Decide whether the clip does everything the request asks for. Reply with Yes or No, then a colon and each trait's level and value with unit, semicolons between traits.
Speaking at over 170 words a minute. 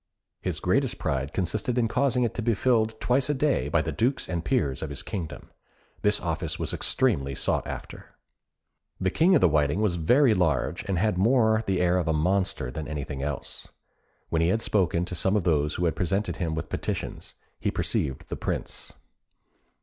Yes: average, 195 wpm